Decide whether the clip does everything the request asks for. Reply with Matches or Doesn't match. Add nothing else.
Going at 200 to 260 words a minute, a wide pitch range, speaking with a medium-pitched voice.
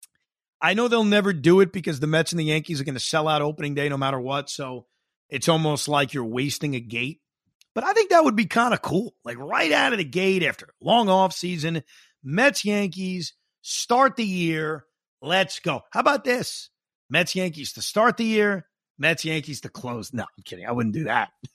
Matches